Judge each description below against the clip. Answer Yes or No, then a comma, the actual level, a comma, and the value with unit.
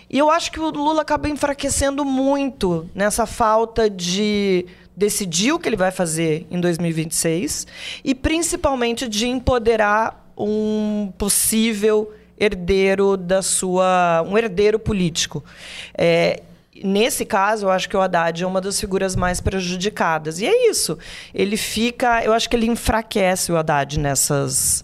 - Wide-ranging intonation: No, average, 4.5 semitones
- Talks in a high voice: Yes, high, 210 Hz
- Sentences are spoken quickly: No, average, 145 wpm